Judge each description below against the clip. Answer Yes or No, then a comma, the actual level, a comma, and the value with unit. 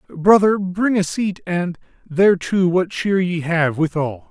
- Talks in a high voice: No, medium, 175 Hz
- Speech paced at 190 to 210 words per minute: No, average, 155 wpm